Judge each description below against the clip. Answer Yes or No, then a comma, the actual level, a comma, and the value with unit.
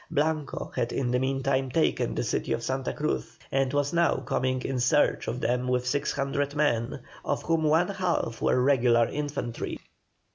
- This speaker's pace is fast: No, average, 175 wpm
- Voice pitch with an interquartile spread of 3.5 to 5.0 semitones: No, average, 2.9 semitones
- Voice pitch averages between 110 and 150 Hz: Yes, low, 135 Hz